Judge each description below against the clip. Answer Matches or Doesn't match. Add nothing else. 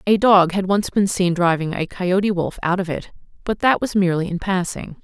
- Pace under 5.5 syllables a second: Matches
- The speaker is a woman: Matches